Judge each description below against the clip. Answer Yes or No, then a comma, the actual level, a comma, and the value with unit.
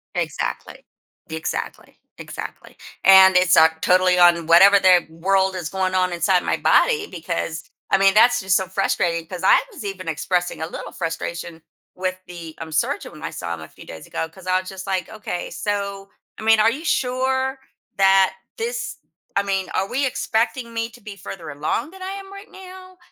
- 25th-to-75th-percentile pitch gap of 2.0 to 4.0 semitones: No, average, 4.5 semitones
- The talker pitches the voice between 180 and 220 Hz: Yes, high, 190 Hz